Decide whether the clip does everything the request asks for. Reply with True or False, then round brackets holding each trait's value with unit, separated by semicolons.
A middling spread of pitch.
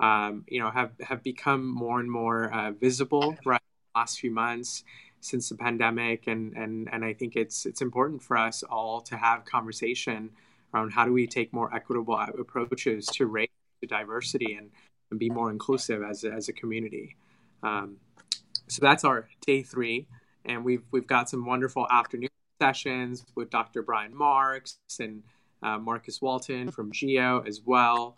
False (2.3 semitones)